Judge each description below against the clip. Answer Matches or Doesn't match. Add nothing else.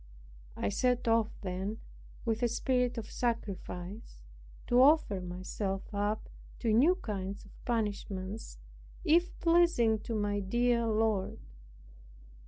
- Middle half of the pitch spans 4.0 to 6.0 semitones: Doesn't match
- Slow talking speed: Matches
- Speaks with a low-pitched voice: Doesn't match